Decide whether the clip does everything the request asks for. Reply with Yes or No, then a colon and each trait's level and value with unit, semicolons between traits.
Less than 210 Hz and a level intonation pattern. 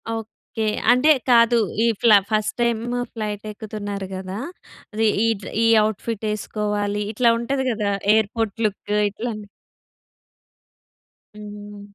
No: high, 215 Hz; narrow, 1.8 semitones